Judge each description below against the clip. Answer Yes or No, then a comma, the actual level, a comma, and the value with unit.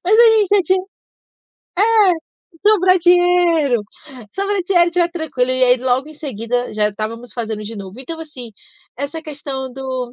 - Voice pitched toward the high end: Yes, very high, 280 Hz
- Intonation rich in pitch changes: Yes, wide, 6.2 semitones